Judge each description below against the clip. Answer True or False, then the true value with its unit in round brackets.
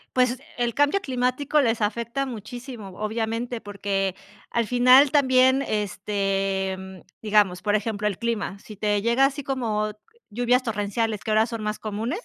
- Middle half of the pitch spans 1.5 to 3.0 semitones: False (3.4 semitones)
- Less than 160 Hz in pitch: False (225 Hz)